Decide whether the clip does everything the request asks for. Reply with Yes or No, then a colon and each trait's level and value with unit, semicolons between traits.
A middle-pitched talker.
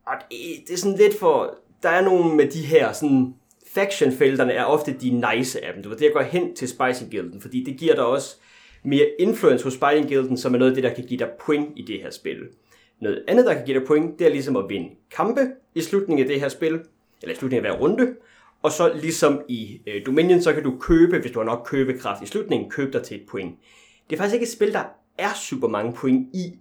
Yes: medium, 160 Hz